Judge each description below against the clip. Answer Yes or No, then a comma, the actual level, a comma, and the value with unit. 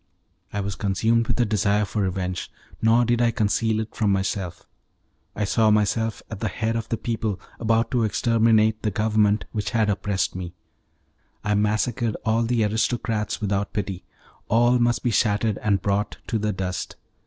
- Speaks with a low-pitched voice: Yes, low, 110 Hz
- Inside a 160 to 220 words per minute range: Yes, average, 170 wpm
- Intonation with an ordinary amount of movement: No, narrow, 2.0 semitones